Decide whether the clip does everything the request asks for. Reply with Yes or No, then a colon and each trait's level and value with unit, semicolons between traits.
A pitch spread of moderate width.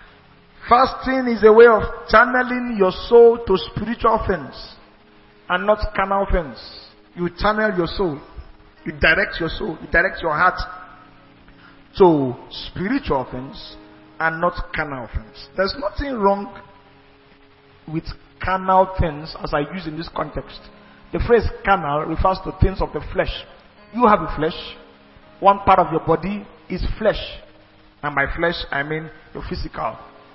No: wide, 6.9 semitones